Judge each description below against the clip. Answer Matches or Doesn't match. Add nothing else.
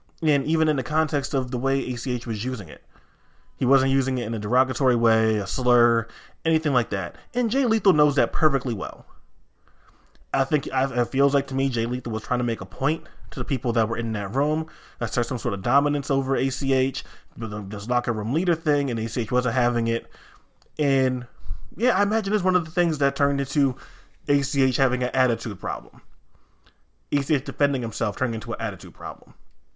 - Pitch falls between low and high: Doesn't match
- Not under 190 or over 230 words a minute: Matches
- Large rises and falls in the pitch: Doesn't match